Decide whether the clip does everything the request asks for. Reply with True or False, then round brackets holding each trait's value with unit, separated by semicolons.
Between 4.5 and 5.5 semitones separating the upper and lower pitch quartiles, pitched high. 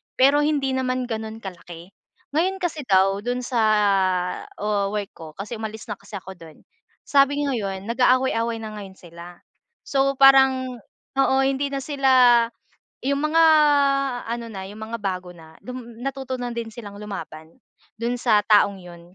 True (5.1 semitones; 230 Hz)